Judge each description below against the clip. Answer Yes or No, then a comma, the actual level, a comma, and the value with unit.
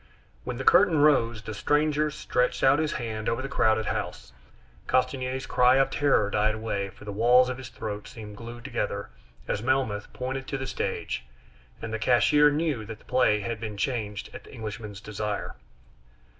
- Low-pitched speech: Yes, low, 120 Hz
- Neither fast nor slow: Yes, average, 180 wpm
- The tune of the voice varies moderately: Yes, average, 3.8 semitones